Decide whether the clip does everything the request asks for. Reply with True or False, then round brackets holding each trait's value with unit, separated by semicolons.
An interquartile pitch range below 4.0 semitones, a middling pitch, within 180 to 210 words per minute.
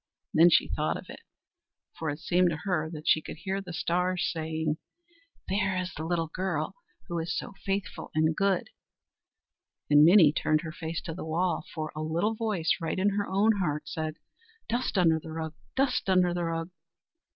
True (3.0 semitones; 170 Hz; 185 wpm)